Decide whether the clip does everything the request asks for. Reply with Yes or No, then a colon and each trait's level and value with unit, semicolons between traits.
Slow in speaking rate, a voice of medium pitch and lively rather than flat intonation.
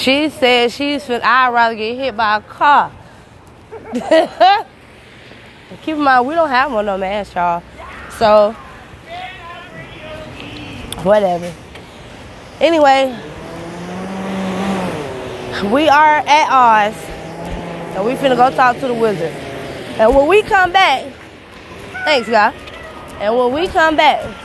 No: slow, 120 wpm; high, 245 Hz; wide, 7.1 semitones